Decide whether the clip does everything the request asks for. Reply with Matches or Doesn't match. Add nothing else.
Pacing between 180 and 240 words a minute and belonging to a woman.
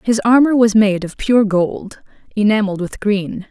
Doesn't match